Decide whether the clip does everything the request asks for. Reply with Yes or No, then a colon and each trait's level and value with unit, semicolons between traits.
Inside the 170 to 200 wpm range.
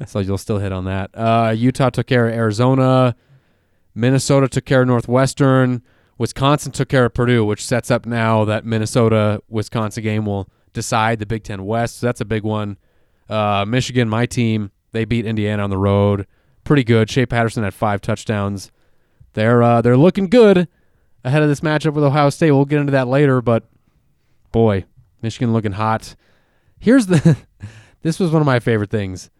Yes: average, 180 wpm